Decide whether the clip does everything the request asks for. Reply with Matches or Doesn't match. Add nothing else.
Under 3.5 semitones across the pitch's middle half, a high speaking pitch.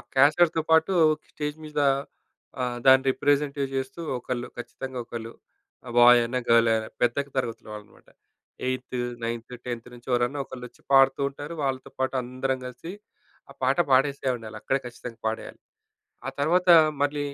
Doesn't match